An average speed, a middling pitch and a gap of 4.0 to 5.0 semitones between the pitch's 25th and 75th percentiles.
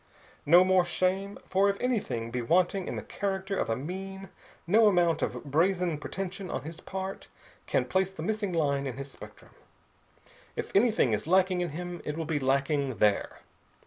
Yes: average, 175 wpm; medium, 180 Hz; average, 4.7 semitones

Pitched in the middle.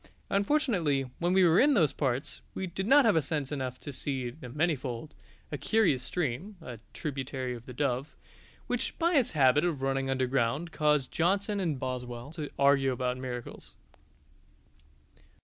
Yes: medium, 145 Hz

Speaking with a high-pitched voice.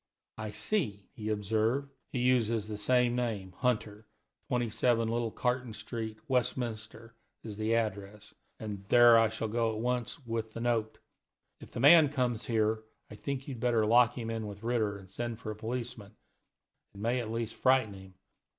No: low, 115 Hz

